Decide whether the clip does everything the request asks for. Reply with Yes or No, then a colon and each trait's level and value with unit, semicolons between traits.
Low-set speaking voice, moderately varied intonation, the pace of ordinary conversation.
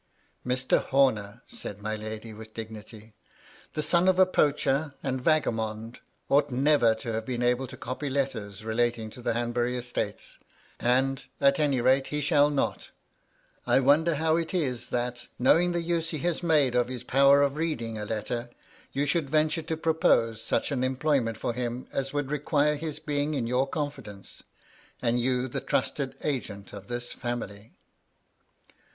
Yes: low, 130 Hz; average, 4.0 semitones; average, 170 wpm